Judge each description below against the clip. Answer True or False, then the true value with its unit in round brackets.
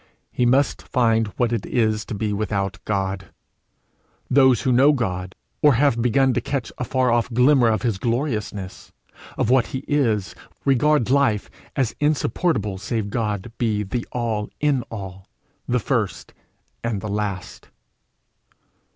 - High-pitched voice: False (115 Hz)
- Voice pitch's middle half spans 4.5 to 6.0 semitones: False (3.8 semitones)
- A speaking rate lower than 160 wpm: True (150 wpm)